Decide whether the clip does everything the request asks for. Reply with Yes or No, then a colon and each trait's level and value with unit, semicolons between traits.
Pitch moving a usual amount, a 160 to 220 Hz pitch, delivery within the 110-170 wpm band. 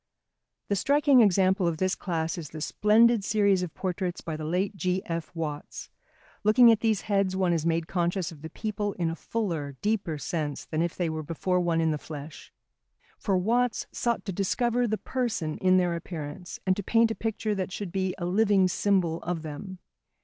No: average, 4.1 semitones; medium, 185 Hz; average, 195 wpm